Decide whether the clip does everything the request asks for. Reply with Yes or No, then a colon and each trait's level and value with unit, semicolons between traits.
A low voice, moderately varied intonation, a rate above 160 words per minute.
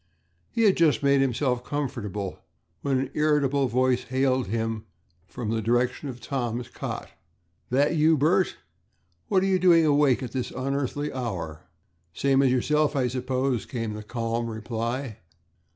No: low, 130 Hz; average, 3.4 semitones; average, 150 wpm